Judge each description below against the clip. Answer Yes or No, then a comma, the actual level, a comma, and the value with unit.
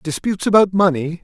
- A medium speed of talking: Yes, average, 145 wpm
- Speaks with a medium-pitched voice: Yes, medium, 175 Hz